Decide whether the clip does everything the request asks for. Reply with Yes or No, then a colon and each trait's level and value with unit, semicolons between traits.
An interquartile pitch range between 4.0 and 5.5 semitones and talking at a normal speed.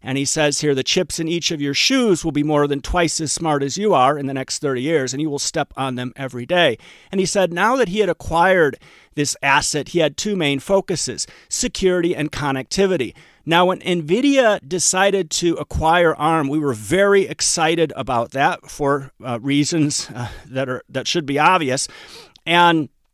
Yes: average, 4.5 semitones; average, 195 wpm